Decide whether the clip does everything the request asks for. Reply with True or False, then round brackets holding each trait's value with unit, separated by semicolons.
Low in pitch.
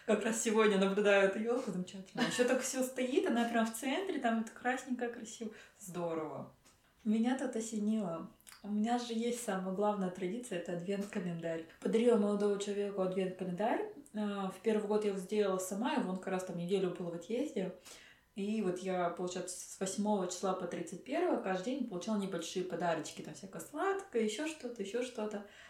False (210 Hz)